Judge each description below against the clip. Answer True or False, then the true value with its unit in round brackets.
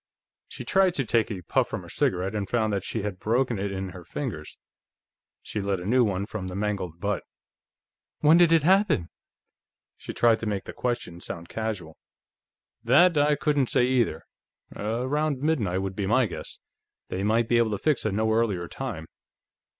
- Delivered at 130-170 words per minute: False (185 wpm)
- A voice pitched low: True (110 Hz)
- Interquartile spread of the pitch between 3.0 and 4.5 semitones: False (5.2 semitones)